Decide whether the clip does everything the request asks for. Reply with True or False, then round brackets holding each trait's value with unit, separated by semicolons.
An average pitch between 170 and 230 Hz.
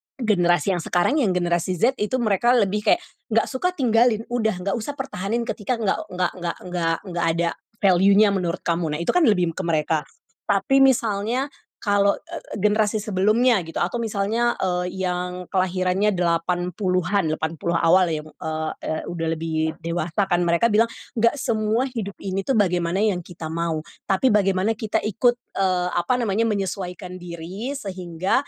True (190 Hz)